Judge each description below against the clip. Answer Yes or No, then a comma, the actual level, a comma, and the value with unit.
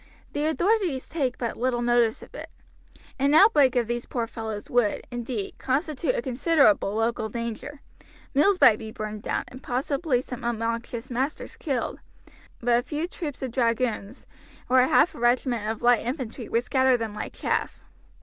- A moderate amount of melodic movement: Yes, average, 3.0 semitones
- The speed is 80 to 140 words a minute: No, average, 165 wpm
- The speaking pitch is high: Yes, high, 245 Hz